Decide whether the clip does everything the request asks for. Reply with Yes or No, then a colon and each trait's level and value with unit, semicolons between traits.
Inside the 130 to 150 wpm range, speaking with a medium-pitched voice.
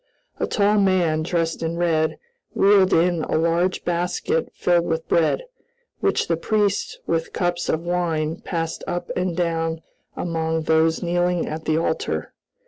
Yes: average, 145 wpm; medium, 170 Hz